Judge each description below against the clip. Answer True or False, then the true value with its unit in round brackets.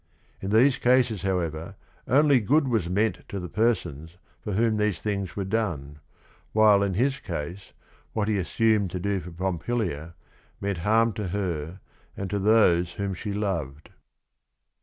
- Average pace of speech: True (160 wpm)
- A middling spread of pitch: True (4.0 semitones)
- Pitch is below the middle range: True (100 Hz)